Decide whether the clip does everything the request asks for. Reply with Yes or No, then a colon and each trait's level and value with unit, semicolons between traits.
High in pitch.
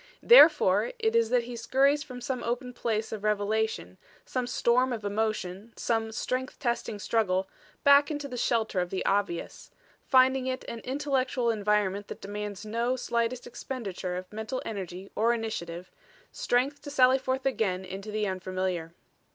Yes: high, 225 Hz